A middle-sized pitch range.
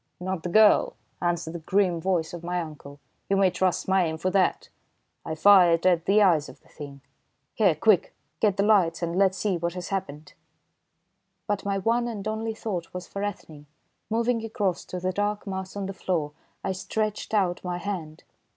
Yes: average, 3.1 semitones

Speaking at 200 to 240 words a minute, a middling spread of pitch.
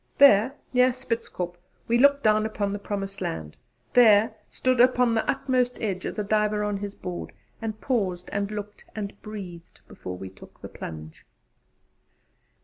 No: average, 155 wpm; average, 3.4 semitones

